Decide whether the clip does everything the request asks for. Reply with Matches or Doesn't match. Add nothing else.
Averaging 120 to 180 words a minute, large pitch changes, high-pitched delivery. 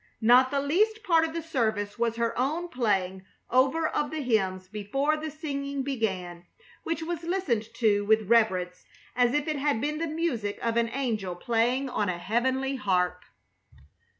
Matches